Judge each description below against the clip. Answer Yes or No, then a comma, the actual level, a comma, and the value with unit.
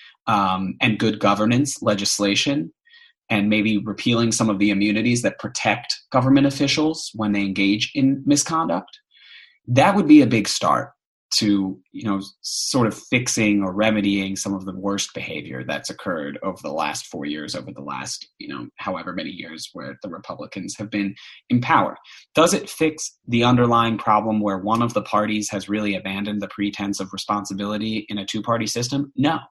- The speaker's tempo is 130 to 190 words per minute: Yes, average, 175 wpm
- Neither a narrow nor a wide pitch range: Yes, average, 3.4 semitones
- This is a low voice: Yes, low, 105 Hz